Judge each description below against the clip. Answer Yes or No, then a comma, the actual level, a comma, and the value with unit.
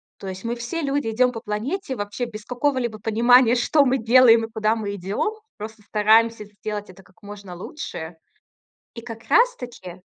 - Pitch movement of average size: Yes, average, 3.2 semitones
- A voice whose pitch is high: Yes, high, 225 Hz